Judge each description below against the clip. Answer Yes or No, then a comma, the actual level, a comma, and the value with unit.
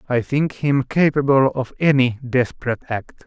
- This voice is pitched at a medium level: No, low, 130 Hz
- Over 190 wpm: No, average, 145 wpm